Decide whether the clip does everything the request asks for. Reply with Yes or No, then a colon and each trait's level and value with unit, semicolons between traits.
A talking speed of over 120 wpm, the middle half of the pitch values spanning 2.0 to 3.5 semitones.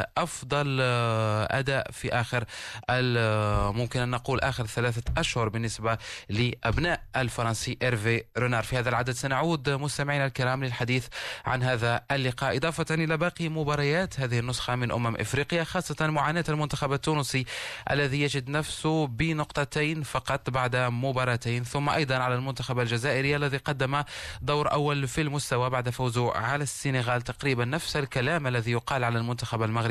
Yes: fast, 135 wpm; average, 3.0 semitones